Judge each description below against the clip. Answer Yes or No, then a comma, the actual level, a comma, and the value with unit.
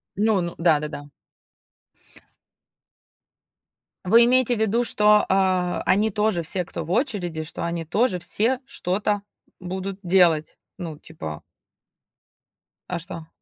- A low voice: No, medium, 185 Hz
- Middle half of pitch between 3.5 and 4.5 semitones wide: Yes, average, 3.9 semitones